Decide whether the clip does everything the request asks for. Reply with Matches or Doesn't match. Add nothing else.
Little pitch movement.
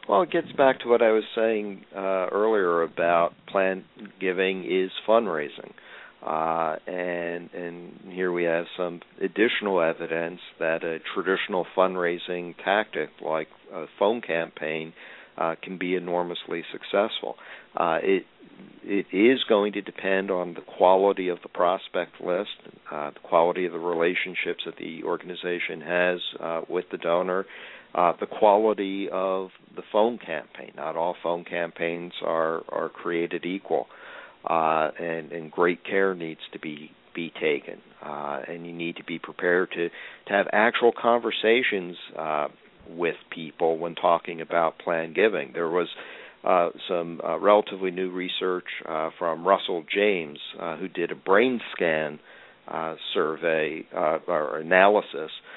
Matches